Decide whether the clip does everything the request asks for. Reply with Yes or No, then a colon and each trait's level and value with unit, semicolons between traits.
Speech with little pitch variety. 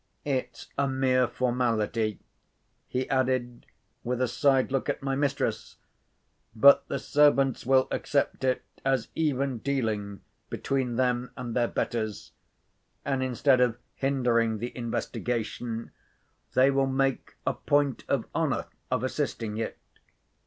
Yes: narrow, 2.3 semitones